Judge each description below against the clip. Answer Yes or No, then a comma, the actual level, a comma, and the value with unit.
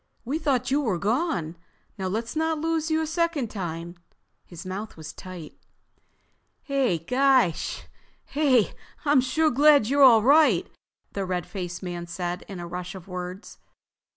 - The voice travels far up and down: Yes, wide, 8.1 semitones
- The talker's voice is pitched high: Yes, high, 220 Hz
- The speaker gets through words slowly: No, average, 145 wpm